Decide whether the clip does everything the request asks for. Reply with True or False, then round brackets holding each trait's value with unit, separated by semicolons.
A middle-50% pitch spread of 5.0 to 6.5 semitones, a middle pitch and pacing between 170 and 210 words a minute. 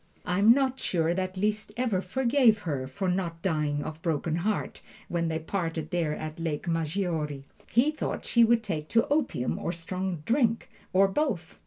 True (5.3 semitones; 180 Hz; 180 wpm)